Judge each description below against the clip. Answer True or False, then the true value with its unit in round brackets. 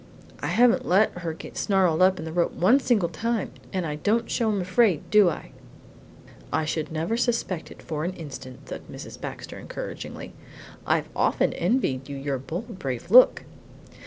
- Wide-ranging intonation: True (5.8 semitones)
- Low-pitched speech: False (180 Hz)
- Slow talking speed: False (175 wpm)